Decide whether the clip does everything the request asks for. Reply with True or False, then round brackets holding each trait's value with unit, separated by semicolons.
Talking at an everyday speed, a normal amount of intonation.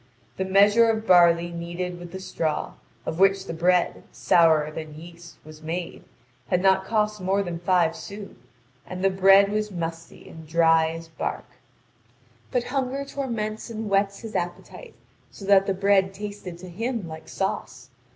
True (165 wpm; 3.2 semitones)